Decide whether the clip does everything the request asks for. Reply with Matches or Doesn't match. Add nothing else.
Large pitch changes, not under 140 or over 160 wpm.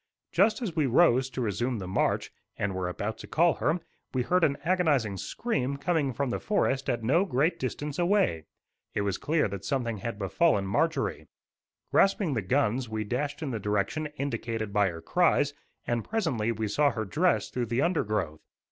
Doesn't match